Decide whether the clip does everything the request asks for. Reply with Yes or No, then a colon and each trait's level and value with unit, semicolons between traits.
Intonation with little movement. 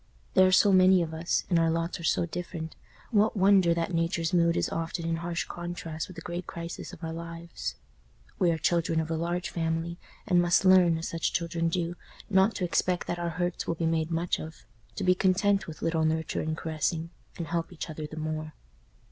Yes: narrow, 1.6 semitones